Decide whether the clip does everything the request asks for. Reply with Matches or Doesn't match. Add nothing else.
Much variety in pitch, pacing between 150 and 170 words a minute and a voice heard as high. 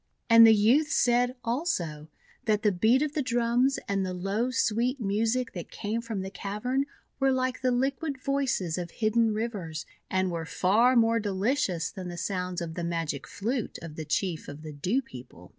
Doesn't match